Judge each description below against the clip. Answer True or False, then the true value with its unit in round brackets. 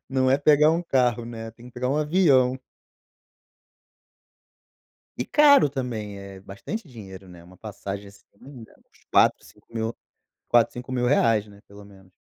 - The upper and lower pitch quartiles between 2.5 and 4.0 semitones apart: False (4.8 semitones)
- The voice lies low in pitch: True (120 Hz)